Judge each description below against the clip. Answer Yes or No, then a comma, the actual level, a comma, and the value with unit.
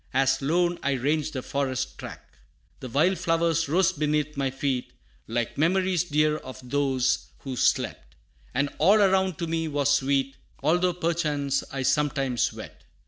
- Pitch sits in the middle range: Yes, medium, 145 Hz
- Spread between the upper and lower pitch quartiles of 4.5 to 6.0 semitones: No, average, 3.6 semitones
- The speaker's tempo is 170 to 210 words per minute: No, average, 150 wpm